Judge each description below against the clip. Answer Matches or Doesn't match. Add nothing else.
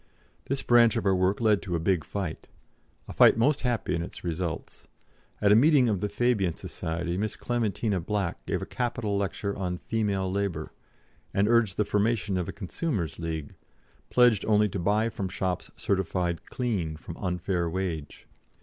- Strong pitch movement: Doesn't match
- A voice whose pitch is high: Doesn't match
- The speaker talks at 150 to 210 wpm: Matches